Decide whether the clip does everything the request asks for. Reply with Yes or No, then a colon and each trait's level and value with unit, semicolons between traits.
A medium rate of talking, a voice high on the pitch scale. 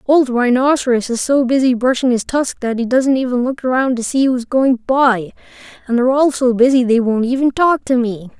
No: fast, 215 wpm; very high, 250 Hz